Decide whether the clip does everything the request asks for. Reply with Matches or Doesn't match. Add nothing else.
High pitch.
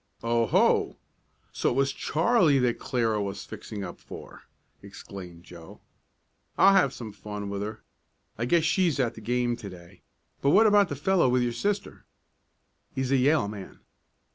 Doesn't match